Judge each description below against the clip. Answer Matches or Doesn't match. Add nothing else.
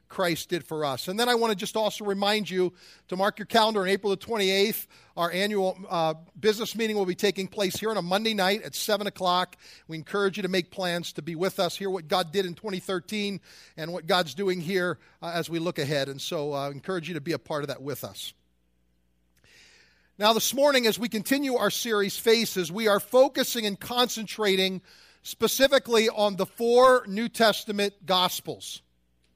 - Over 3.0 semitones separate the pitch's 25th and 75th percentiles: Matches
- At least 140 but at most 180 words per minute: Doesn't match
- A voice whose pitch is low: Doesn't match